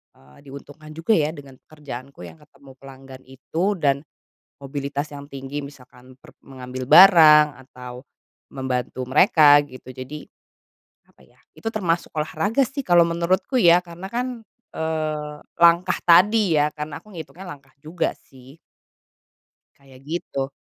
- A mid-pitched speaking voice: Yes, medium, 150 Hz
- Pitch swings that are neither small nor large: Yes, average, 4.0 semitones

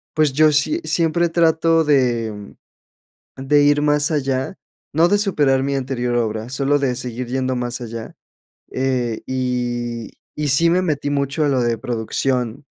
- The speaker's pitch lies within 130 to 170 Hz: Yes, low, 135 Hz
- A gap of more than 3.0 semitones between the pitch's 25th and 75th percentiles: Yes, average, 3.5 semitones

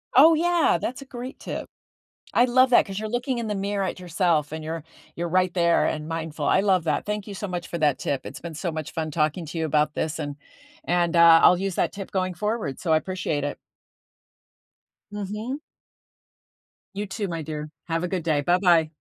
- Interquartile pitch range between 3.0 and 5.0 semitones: Yes, average, 4.4 semitones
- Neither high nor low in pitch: Yes, medium, 175 Hz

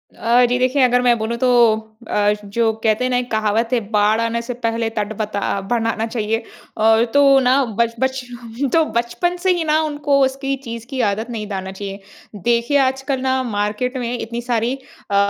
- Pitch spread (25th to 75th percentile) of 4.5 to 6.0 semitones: No, average, 2.7 semitones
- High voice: Yes, high, 235 Hz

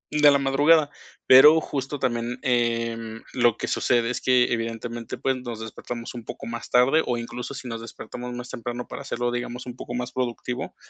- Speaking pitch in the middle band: No, low, 120 Hz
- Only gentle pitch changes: Yes, narrow, 1.8 semitones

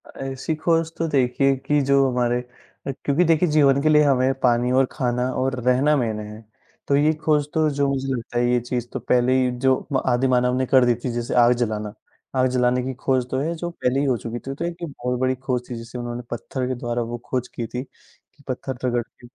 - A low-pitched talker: Yes, low, 130 Hz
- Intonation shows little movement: Yes, narrow, 2.2 semitones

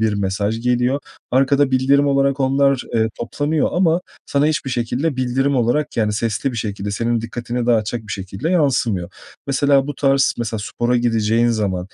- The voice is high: No, low, 120 Hz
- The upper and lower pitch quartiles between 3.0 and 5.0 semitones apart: Yes, average, 3.7 semitones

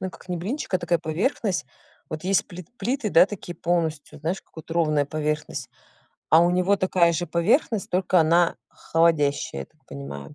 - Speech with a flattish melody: No, average, 3.0 semitones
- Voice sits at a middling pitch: Yes, medium, 170 Hz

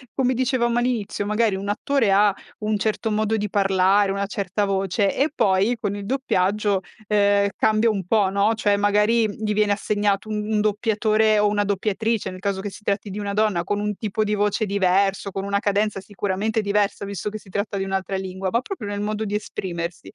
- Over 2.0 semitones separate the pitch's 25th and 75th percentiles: No, narrow, 1.5 semitones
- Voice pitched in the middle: No, high, 205 Hz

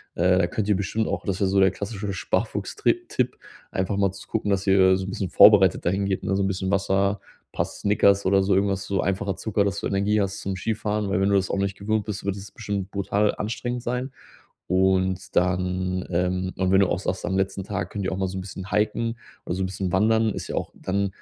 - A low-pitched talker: Yes, very low, 95 Hz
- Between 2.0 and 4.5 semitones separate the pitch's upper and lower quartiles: No, narrow, 1.4 semitones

